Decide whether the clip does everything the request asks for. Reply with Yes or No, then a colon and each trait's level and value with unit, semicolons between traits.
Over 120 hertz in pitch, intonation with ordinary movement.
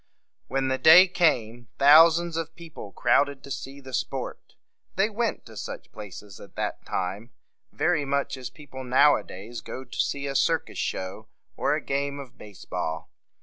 Yes: low, 135 Hz; average, 5.0 semitones